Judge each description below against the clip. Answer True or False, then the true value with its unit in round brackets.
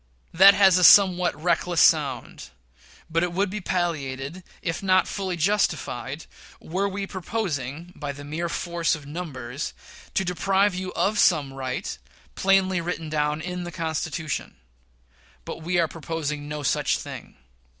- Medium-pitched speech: True (170 Hz)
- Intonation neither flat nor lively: True (3.8 semitones)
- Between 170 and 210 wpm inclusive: False (145 wpm)